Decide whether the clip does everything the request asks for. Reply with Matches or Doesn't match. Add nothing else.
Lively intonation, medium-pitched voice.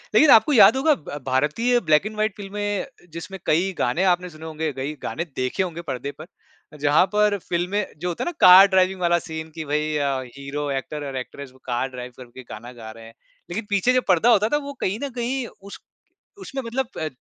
Matches